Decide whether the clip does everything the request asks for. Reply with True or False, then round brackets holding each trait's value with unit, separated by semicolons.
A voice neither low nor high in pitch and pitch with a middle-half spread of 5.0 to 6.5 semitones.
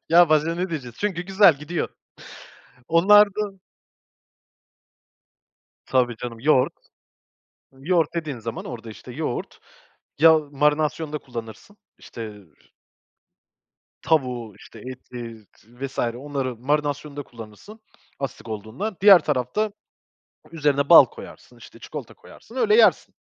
True (145 Hz; 5.5 semitones)